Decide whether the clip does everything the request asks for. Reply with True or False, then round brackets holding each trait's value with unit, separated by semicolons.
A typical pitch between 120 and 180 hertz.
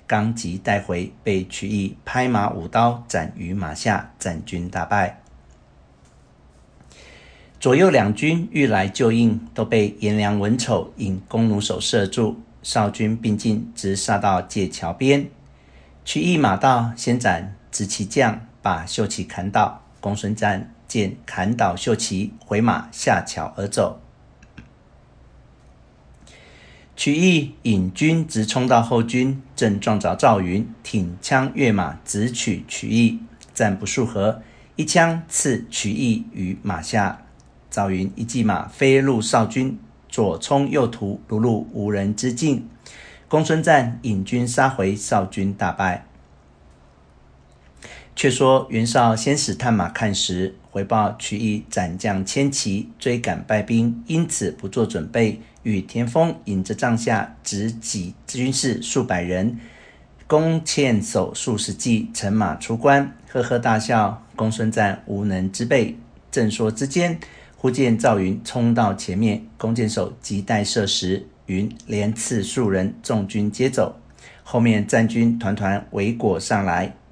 False (110 Hz)